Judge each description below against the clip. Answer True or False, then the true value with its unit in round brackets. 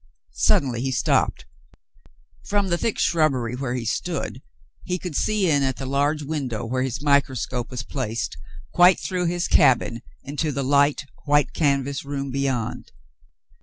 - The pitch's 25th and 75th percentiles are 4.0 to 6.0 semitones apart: False (3.2 semitones)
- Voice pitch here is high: False (140 Hz)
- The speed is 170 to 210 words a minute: False (150 wpm)